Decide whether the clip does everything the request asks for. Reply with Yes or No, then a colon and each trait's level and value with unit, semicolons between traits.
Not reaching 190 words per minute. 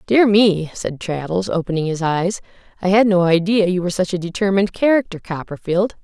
Yes: average, 180 wpm